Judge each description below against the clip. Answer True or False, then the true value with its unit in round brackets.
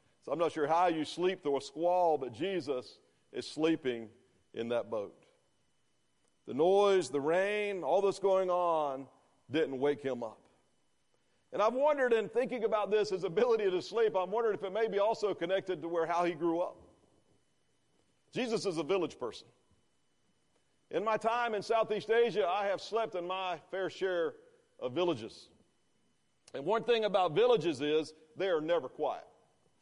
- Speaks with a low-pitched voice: False (190 Hz)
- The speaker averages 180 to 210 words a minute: False (165 wpm)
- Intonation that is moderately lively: False (5.7 semitones)